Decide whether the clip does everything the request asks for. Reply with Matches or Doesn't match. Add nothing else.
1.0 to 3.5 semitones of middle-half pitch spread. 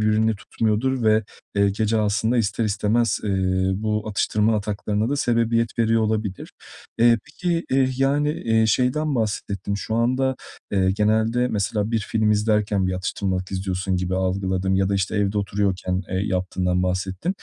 Matches